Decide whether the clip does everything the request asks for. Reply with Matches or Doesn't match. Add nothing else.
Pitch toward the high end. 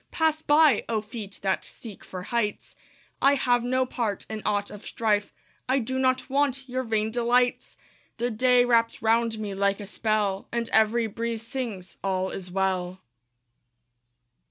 Matches